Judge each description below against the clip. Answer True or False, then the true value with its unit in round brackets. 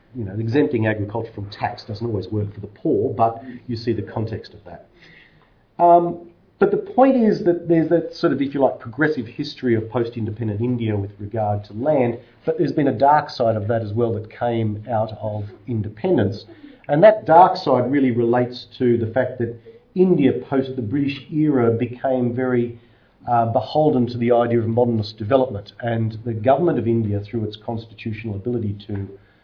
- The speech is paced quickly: False (185 wpm)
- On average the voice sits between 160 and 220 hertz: False (120 Hz)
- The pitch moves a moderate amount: True (3.7 semitones)